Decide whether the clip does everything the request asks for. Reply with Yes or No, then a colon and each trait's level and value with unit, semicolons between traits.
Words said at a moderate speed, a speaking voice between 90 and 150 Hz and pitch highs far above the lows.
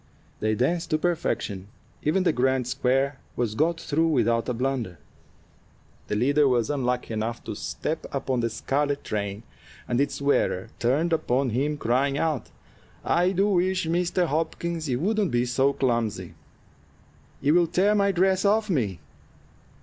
Yes: average, 150 wpm; medium, 140 Hz; wide, 5.7 semitones